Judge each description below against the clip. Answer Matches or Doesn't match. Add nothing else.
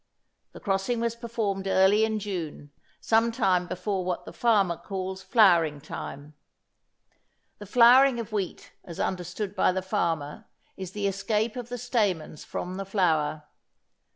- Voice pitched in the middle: Doesn't match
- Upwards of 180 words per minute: Doesn't match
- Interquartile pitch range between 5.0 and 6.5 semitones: Doesn't match